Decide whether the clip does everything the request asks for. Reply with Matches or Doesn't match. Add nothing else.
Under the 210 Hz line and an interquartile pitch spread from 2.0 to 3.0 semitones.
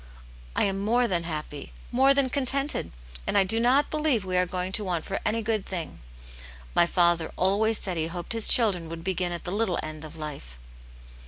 Doesn't match